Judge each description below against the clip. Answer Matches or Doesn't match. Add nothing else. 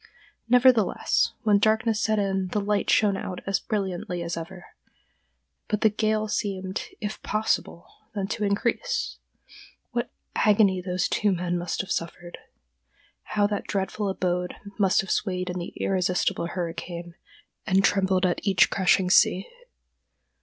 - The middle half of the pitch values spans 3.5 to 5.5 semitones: Doesn't match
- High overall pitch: Matches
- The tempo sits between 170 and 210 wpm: Doesn't match